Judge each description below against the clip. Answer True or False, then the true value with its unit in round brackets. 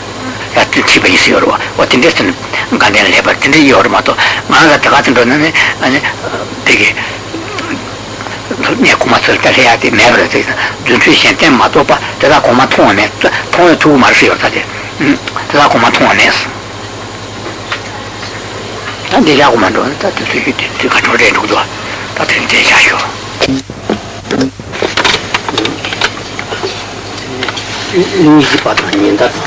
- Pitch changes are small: False (4.1 semitones)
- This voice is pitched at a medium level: False (105 Hz)